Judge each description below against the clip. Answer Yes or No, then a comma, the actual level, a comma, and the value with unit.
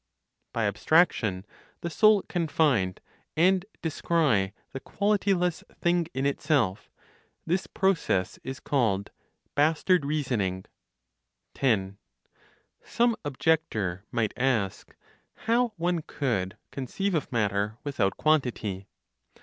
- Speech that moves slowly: Yes, slow, 100 wpm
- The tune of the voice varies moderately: No, wide, 8.8 semitones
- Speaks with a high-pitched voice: No, medium, 140 Hz